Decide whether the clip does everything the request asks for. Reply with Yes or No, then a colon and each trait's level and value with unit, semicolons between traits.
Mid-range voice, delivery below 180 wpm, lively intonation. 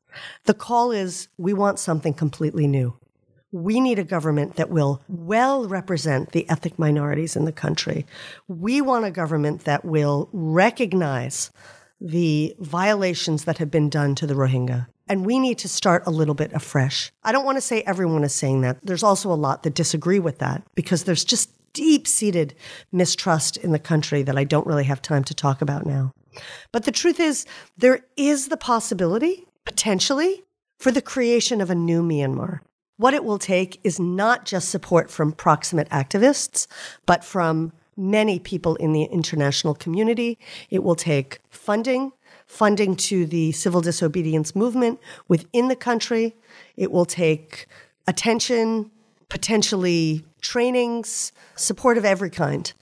Yes: medium, 180 Hz; average, 160 wpm; wide, 6.2 semitones